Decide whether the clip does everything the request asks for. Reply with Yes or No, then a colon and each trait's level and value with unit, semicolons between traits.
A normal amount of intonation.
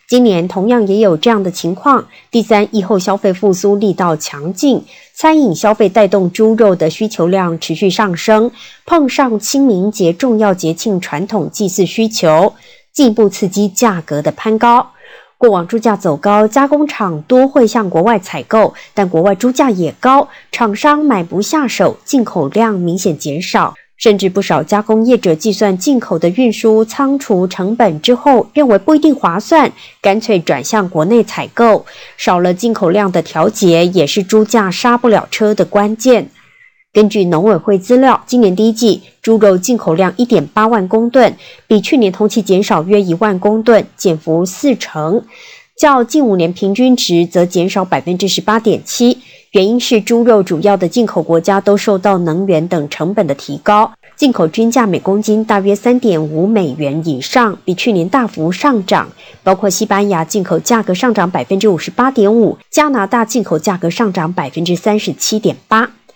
Yes: average, 4.2 semitones